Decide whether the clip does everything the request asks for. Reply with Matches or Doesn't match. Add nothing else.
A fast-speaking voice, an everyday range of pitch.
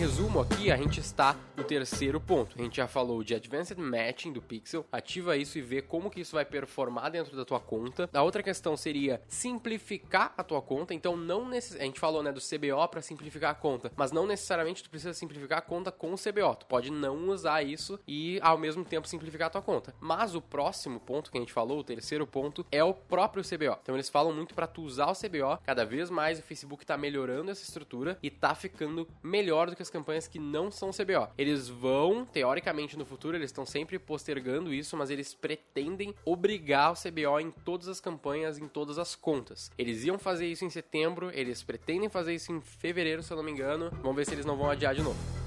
Matches